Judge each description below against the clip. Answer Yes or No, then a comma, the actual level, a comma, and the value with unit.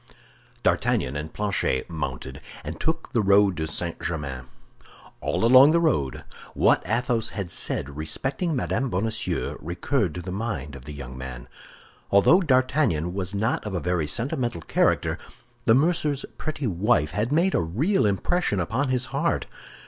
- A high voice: No, low, 100 Hz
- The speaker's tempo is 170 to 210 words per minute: No, average, 155 wpm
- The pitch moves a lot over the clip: Yes, wide, 8.5 semitones